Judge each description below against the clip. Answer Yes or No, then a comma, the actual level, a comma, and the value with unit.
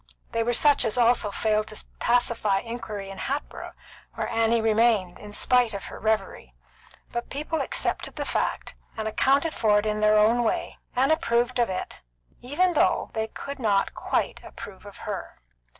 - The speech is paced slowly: No, average, 165 wpm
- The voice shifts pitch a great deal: No, narrow, 2.6 semitones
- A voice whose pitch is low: No, high, 230 Hz